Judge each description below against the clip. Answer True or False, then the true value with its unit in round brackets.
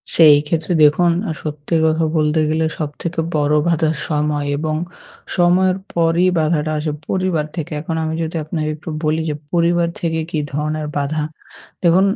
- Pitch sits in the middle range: True (160 Hz)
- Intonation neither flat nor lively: False (2.0 semitones)